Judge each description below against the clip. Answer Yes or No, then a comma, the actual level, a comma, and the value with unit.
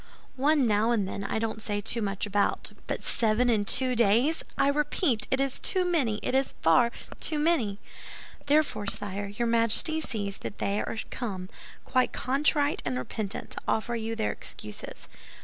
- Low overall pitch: No, high, 225 Hz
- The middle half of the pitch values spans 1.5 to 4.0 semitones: No, average, 4.8 semitones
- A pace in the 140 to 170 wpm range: Yes, average, 165 wpm